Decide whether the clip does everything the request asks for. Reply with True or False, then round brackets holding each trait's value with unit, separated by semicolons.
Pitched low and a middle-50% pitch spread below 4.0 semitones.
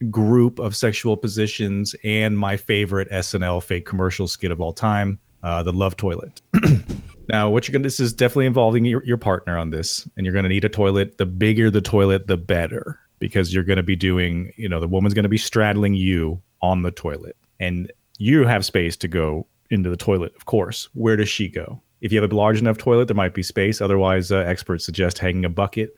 True (100 Hz; 3.1 semitones)